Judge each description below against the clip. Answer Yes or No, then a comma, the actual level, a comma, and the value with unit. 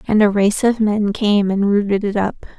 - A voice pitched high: Yes, high, 205 Hz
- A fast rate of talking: Yes, fast, 230 wpm